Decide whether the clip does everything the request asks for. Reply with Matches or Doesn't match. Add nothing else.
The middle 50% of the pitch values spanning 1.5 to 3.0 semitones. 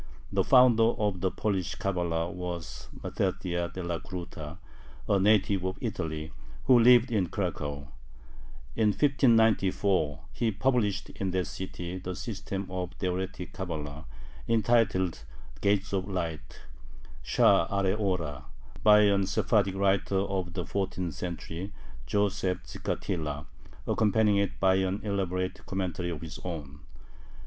Matches